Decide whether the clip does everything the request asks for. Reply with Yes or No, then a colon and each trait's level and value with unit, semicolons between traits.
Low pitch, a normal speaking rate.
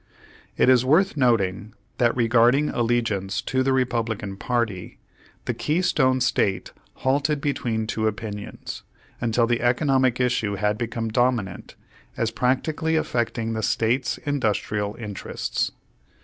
No: low, 120 Hz; slow, 120 wpm